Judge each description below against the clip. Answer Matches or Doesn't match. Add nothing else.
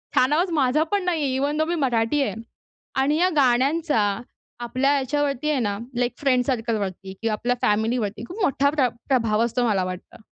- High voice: Matches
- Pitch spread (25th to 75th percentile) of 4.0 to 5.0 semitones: Matches